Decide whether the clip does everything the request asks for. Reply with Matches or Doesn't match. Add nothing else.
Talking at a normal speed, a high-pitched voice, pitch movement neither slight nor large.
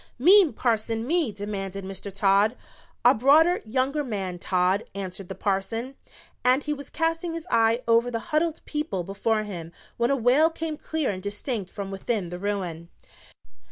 Doesn't match